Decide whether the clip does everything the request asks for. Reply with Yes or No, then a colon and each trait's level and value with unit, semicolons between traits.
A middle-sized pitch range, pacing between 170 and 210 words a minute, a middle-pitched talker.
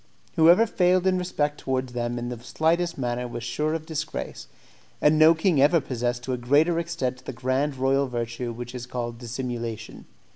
No: average, 4.7 semitones; average, 180 wpm; low, 130 Hz